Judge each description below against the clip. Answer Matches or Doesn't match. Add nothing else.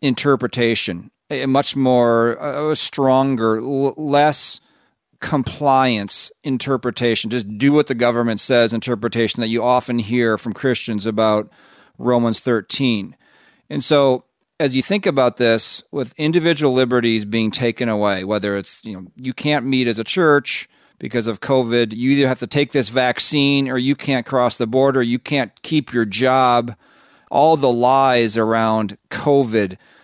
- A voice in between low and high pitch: Doesn't match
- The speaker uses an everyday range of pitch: Matches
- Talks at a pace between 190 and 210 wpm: Doesn't match